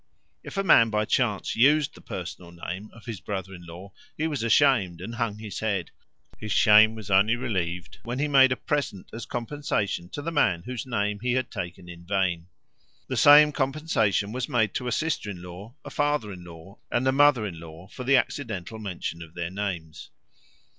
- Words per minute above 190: Yes, average, 200 wpm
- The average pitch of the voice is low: Yes, low, 110 Hz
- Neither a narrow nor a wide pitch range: No, wide, 5.9 semitones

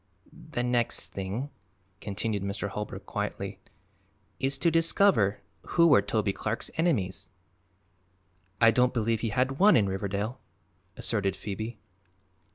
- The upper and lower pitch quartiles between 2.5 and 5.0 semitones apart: Yes, average, 4.3 semitones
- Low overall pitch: Yes, low, 110 Hz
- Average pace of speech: No, slow, 120 wpm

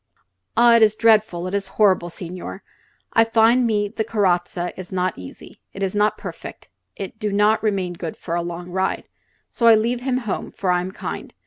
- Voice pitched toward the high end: Yes, high, 200 Hz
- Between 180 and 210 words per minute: Yes, average, 200 wpm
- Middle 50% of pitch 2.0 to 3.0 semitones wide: No, average, 3.5 semitones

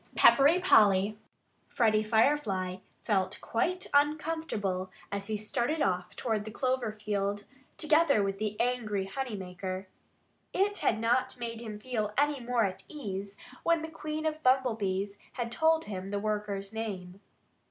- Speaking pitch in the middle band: No, high, 215 Hz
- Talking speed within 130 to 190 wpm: Yes, average, 145 wpm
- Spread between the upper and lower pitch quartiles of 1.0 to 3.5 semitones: No, average, 5.2 semitones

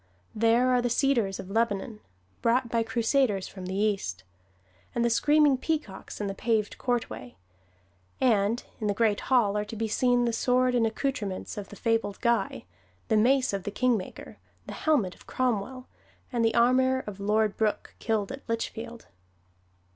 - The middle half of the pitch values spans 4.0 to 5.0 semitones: No, average, 3.4 semitones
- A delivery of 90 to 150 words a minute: No, average, 165 wpm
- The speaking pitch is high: Yes, high, 230 Hz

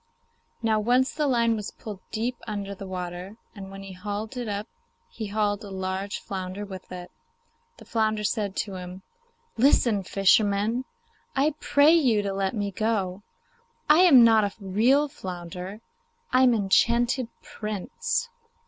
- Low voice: No, high, 210 Hz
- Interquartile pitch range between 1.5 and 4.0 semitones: Yes, average, 3.4 semitones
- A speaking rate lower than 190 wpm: Yes, average, 155 wpm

